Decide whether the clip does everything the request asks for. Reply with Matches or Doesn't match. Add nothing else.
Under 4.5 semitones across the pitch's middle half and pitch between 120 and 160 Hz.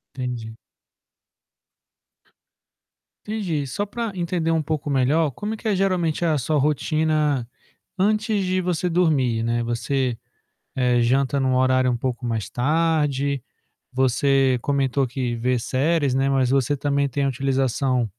Matches